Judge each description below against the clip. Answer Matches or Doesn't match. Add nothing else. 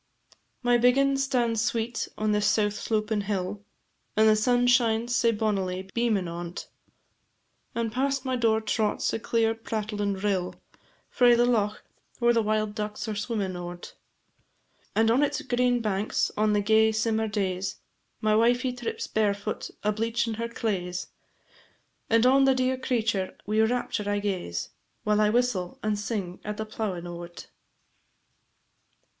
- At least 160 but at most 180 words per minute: Doesn't match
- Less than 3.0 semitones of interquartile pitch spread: Matches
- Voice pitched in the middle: Doesn't match